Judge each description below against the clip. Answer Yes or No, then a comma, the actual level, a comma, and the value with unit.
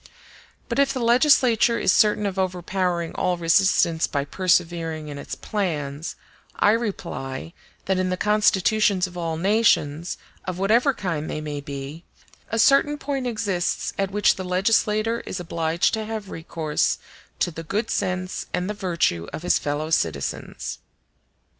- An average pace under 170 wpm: Yes, average, 150 wpm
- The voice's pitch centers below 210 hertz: Yes, medium, 185 Hz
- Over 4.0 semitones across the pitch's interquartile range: Yes, average, 4.5 semitones